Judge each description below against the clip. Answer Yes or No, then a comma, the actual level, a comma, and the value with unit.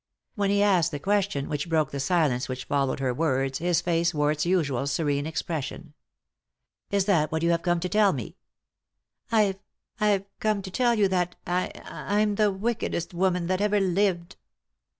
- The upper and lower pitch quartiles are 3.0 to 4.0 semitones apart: No, average, 4.8 semitones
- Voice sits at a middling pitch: Yes, medium, 175 Hz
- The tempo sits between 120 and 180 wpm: No, average, 190 wpm